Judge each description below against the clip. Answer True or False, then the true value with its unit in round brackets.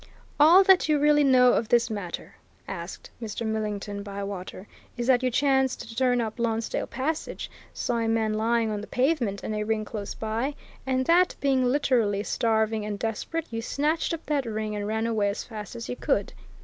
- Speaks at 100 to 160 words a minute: False (190 wpm)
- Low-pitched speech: False (230 Hz)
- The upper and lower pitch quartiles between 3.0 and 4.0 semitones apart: True (3.7 semitones)